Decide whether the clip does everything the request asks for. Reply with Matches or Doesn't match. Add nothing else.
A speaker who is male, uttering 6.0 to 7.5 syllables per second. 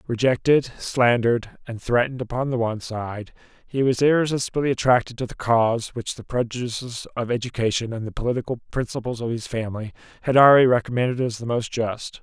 Matches